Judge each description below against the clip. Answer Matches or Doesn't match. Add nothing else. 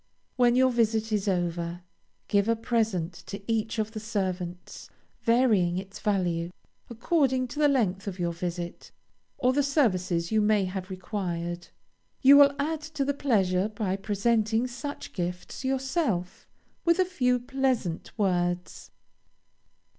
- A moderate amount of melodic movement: Doesn't match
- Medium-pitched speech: Doesn't match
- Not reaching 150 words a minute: Matches